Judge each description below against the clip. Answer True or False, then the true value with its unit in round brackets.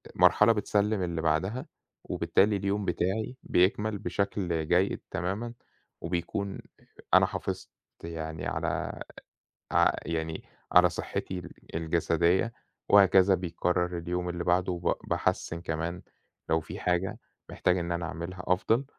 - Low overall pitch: True (90 Hz)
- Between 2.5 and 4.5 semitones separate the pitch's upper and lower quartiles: True (2.8 semitones)